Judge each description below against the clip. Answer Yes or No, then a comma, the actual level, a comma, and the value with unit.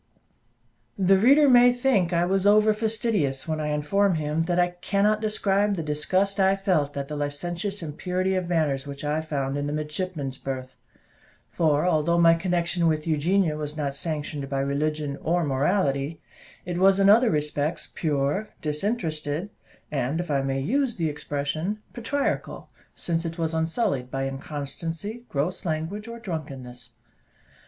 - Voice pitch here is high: No, medium, 165 Hz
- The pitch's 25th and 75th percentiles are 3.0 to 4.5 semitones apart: No, average, 4.9 semitones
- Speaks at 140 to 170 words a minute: Yes, average, 155 wpm